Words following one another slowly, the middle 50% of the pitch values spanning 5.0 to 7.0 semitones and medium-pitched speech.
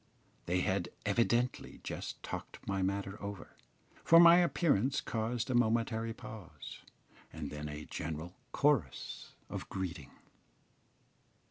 No: slow, 115 wpm; wide, 5.5 semitones; low, 100 Hz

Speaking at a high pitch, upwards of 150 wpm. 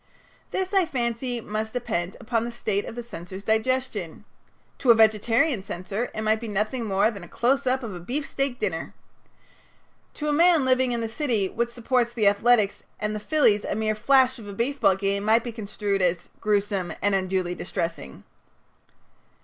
Yes: high, 220 Hz; average, 180 wpm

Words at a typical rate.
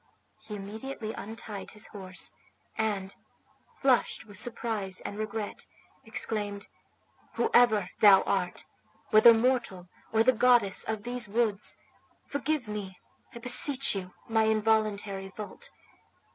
No: slow, 115 wpm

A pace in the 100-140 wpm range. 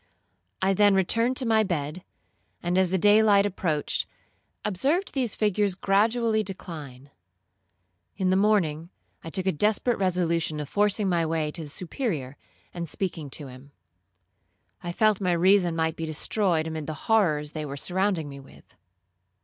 No: average, 155 wpm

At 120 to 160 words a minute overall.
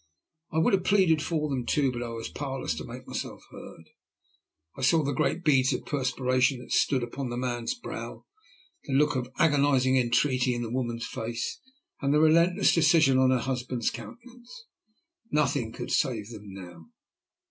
No: average, 170 wpm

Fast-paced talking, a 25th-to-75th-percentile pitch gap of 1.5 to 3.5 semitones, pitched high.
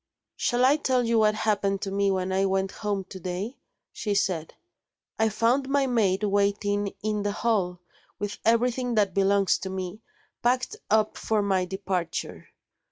No: average, 165 wpm; average, 2.9 semitones; high, 205 Hz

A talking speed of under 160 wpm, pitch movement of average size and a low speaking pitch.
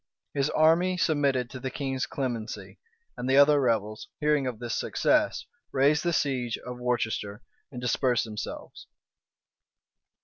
Yes: slow, 135 wpm; average, 3.1 semitones; low, 130 Hz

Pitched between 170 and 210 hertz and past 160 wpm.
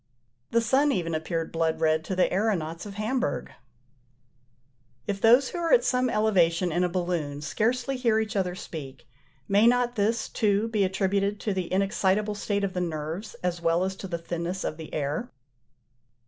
Yes: high, 190 Hz; average, 175 wpm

